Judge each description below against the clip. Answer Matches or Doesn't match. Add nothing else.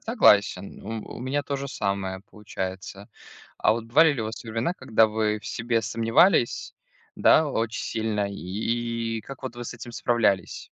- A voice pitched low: Matches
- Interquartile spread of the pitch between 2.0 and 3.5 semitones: Matches